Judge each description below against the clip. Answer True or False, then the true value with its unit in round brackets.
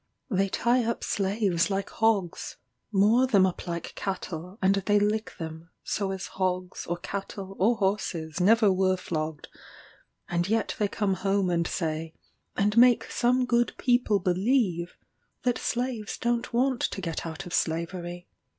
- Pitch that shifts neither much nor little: True (3.9 semitones)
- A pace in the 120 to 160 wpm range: True (150 wpm)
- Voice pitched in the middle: False (195 Hz)